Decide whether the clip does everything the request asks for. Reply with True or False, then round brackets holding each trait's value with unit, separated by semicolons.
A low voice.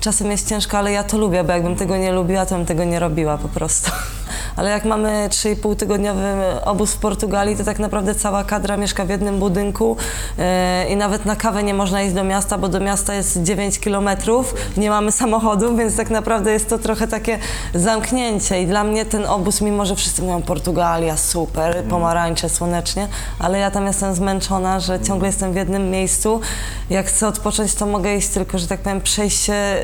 False (200 Hz)